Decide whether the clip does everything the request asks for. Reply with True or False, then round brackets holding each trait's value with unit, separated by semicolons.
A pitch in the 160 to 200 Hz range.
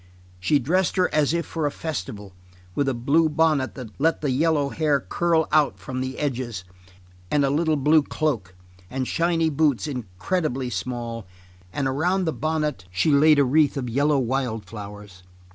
False (140 Hz)